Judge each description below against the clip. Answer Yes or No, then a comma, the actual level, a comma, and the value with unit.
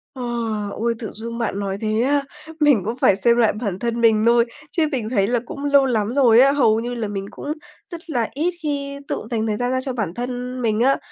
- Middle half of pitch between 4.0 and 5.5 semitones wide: No, average, 3.4 semitones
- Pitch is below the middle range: No, high, 235 Hz